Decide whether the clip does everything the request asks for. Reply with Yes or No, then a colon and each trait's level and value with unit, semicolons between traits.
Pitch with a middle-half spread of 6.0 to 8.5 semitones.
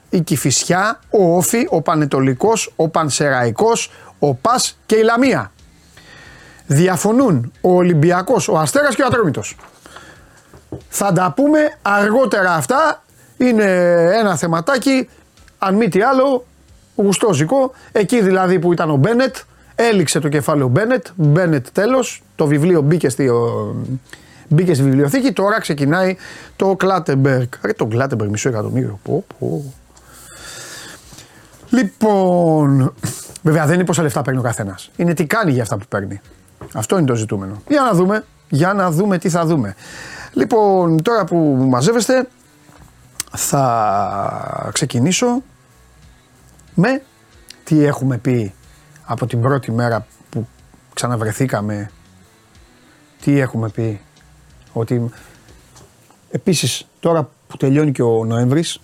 Yes: wide, 7.6 semitones